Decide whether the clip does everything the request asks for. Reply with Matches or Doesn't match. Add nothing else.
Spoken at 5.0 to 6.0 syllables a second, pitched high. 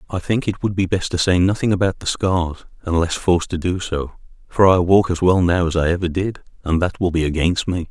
Doesn't match